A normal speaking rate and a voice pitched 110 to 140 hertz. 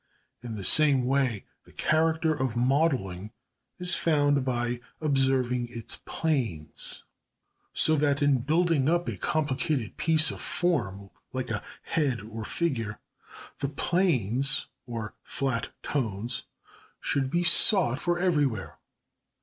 No: slow, 120 wpm; low, 135 Hz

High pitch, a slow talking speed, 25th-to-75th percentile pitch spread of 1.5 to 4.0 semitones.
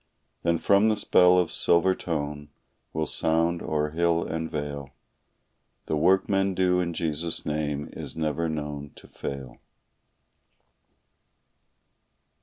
No: very low, 80 Hz; slow, 120 wpm; average, 2.9 semitones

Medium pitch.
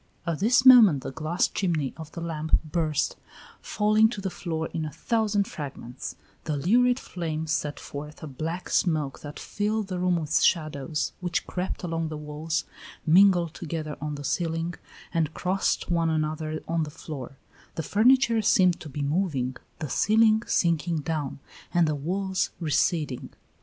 Yes: medium, 165 Hz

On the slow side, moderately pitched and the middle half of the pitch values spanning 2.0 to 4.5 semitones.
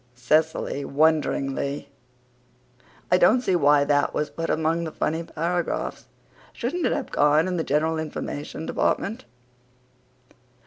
Yes: slow, 125 wpm; medium, 160 Hz; narrow, 2.6 semitones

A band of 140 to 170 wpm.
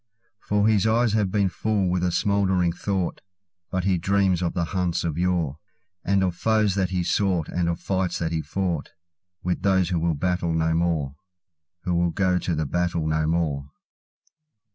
Yes: average, 165 wpm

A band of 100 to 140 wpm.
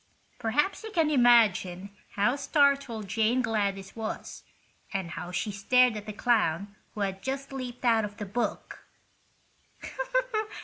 Yes: slow, 135 wpm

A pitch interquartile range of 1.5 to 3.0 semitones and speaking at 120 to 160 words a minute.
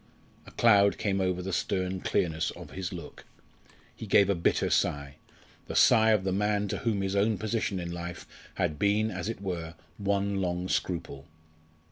No: narrow, 2.5 semitones; average, 175 wpm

